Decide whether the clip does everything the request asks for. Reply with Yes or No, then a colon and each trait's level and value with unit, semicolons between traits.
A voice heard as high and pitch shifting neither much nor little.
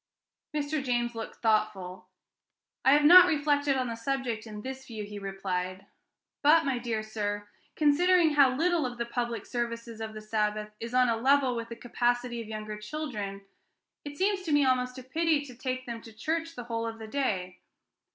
Yes: high, 240 Hz; average, 4.7 semitones